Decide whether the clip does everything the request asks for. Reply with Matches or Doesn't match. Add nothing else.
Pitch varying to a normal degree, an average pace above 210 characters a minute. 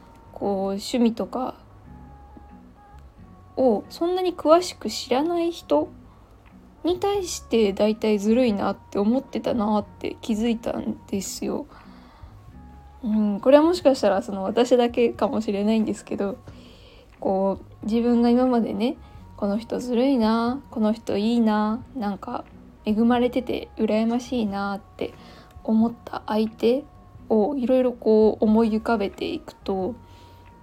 Matches